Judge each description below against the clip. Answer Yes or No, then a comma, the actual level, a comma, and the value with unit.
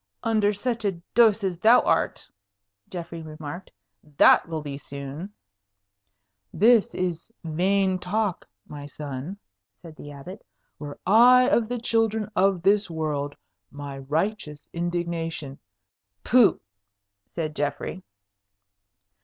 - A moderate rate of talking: No, slow, 115 wpm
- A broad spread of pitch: Yes, wide, 5.9 semitones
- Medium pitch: Yes, medium, 175 Hz